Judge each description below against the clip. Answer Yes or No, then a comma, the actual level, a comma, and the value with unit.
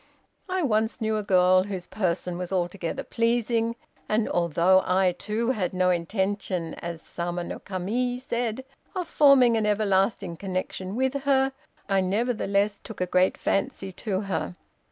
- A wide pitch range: No, average, 4.1 semitones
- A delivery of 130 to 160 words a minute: Yes, average, 150 wpm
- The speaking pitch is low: No, high, 200 Hz